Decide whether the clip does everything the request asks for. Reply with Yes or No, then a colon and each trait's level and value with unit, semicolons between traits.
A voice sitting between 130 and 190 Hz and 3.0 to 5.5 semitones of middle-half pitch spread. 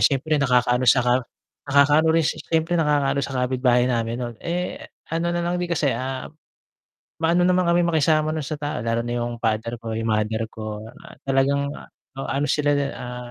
Yes: low, 135 Hz; average, 4.6 semitones